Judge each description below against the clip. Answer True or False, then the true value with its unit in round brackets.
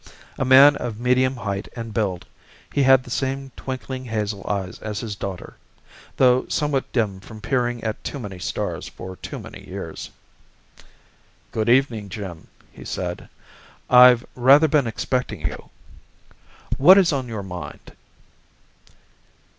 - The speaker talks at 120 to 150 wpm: True (140 wpm)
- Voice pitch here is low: True (120 Hz)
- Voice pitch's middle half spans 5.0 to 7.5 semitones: False (4.3 semitones)